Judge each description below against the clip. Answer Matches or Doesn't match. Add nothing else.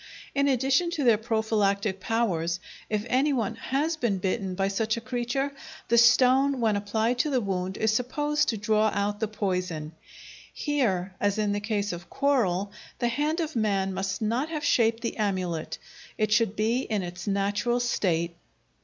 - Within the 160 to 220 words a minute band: Matches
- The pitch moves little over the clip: Doesn't match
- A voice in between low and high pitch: Doesn't match